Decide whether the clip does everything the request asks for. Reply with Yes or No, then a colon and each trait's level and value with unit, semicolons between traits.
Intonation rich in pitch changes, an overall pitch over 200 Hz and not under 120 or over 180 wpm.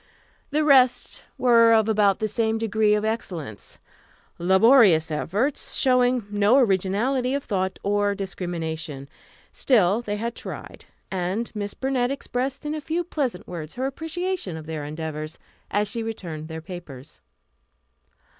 Yes: wide, 6.0 semitones; high, 210 Hz; slow, 135 wpm